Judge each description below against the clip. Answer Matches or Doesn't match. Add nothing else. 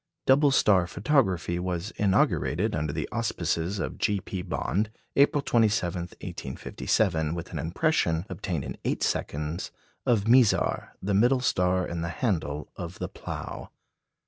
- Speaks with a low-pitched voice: Matches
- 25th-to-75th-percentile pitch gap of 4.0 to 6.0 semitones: Matches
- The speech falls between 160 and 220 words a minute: Doesn't match